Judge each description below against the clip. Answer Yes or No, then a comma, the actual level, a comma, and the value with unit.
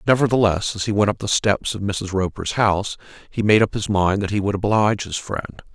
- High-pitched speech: No, low, 100 Hz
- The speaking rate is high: Yes, fast, 230 wpm